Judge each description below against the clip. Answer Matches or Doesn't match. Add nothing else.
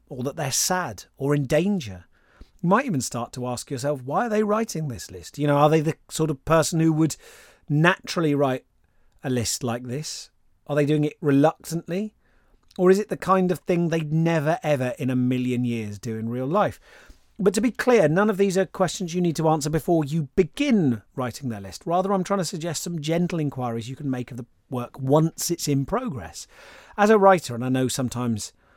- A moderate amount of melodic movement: Doesn't match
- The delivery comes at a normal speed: Doesn't match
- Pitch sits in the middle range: Matches